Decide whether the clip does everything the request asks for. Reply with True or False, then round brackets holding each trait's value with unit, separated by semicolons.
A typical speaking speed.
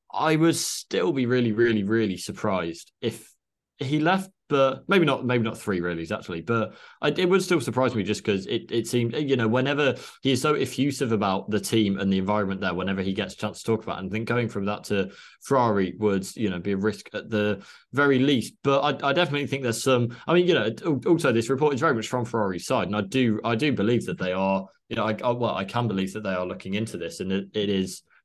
False (255 wpm)